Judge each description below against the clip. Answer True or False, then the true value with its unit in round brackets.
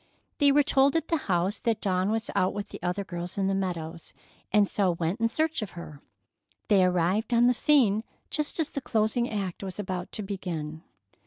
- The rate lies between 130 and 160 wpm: False (200 wpm)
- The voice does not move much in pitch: False (4.6 semitones)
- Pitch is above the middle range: True (200 Hz)